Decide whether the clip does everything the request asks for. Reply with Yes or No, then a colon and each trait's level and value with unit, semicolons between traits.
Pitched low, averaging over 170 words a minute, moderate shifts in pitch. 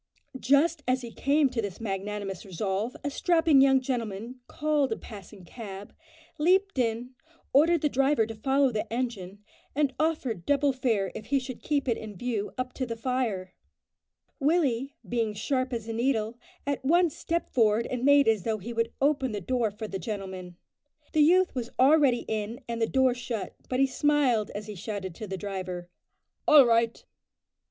No: high, 240 Hz; average, 180 wpm; average, 4.5 semitones